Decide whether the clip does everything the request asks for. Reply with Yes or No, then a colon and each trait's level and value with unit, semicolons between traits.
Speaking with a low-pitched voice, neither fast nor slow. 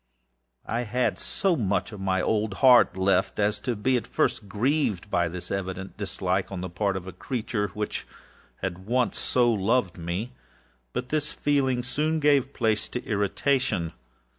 Yes: low, 105 Hz; average, 165 wpm